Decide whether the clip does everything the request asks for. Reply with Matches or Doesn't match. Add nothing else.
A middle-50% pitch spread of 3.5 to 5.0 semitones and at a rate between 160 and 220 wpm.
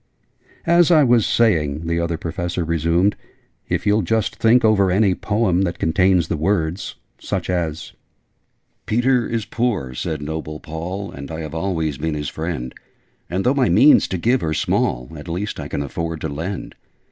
Matches